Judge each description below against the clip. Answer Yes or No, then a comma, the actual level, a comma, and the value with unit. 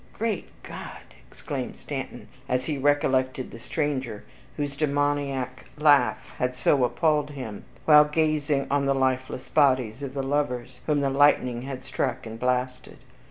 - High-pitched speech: No, low, 135 Hz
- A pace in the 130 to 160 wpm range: Yes, average, 150 wpm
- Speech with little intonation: Yes, narrow, 2.3 semitones